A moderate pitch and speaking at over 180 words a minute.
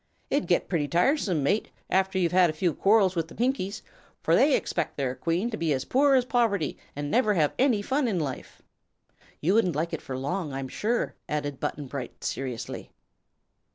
Yes: medium, 180 Hz; average, 190 wpm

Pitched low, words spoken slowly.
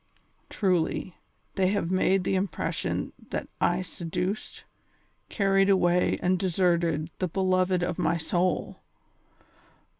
No: medium, 185 Hz; slow, 110 wpm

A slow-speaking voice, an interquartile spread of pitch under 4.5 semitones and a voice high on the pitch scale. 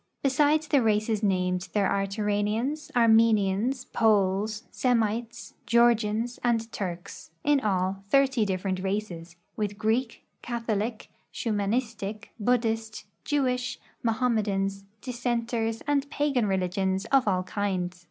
Yes: slow, 115 wpm; average, 3.5 semitones; high, 220 Hz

